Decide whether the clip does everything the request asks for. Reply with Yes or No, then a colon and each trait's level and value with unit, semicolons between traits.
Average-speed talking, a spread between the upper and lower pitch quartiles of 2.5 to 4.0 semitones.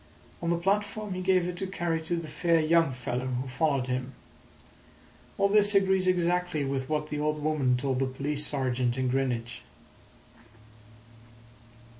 No: average, 155 wpm; average, 5.3 semitones